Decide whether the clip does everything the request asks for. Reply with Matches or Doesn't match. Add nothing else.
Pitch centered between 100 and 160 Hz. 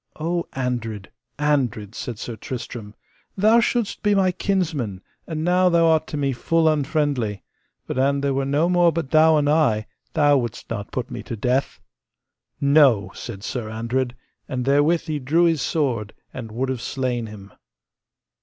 Matches